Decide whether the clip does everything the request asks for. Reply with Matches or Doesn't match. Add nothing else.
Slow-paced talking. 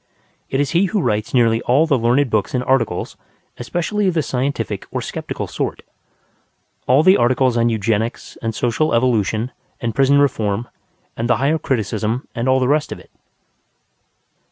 Doesn't match